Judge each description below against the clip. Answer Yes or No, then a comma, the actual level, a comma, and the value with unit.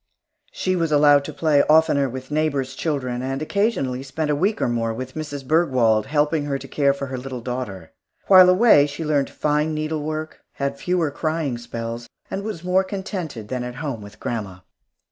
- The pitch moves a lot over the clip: No, average, 3.7 semitones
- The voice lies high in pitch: No, medium, 145 Hz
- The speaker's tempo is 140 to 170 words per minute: No, average, 185 wpm